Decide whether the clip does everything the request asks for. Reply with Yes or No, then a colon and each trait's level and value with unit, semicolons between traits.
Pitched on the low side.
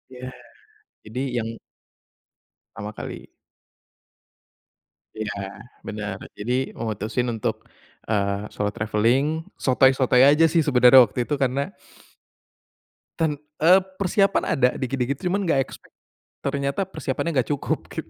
Yes: low, 130 Hz